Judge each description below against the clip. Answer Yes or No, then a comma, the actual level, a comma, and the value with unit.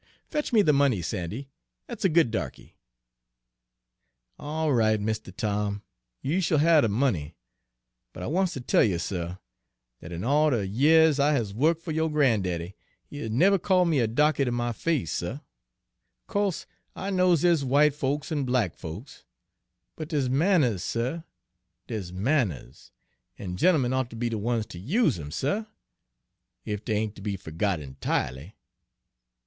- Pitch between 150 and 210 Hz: No, low, 125 Hz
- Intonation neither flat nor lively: No, wide, 7.2 semitones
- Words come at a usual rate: Yes, average, 160 wpm